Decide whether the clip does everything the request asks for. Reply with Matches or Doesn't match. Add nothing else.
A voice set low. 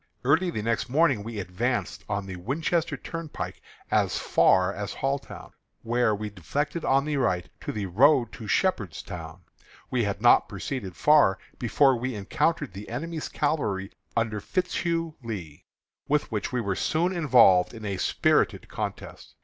Matches